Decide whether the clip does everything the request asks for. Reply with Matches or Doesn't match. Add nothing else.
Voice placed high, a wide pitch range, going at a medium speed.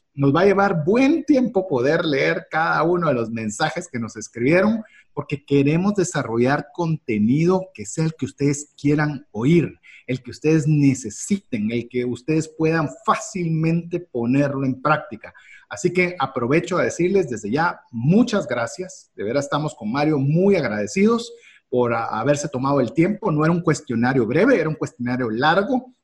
Doesn't match